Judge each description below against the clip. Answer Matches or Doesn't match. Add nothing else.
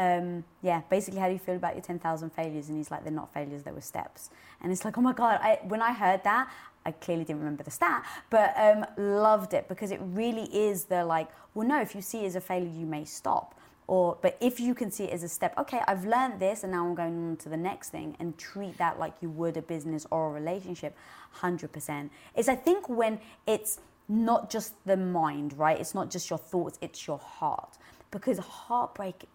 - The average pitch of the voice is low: Doesn't match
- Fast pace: Matches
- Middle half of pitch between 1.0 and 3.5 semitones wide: Doesn't match